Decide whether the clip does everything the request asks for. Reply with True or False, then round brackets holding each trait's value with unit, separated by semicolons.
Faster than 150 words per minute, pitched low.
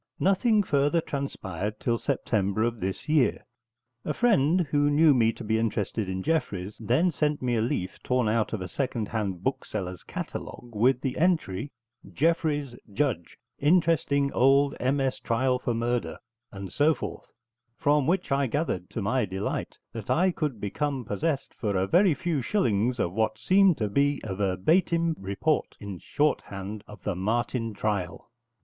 True (160 wpm; 125 Hz)